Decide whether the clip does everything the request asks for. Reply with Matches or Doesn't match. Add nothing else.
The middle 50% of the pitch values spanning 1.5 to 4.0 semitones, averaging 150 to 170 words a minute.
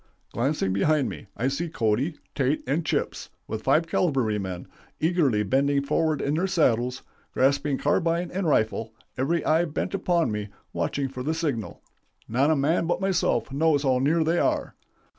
Doesn't match